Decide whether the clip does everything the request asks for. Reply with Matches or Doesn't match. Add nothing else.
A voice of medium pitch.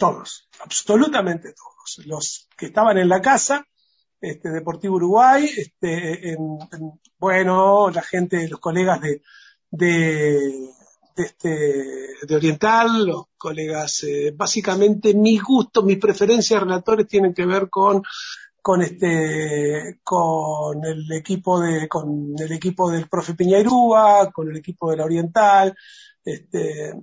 Matches